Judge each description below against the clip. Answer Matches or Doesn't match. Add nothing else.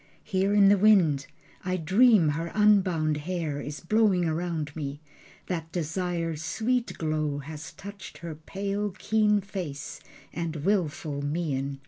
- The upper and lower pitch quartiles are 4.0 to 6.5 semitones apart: Matches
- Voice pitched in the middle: Matches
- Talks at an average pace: Doesn't match